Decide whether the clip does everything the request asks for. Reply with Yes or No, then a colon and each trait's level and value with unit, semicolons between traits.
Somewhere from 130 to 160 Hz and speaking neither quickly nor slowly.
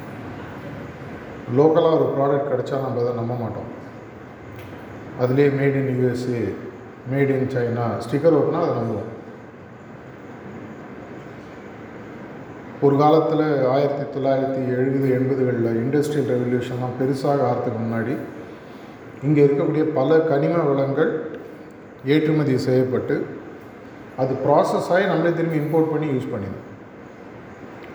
Yes: low, 135 Hz; average, 100 wpm